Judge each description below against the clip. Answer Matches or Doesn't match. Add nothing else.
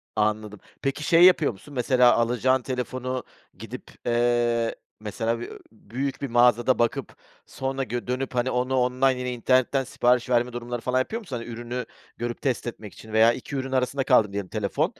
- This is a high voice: Doesn't match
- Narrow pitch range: Matches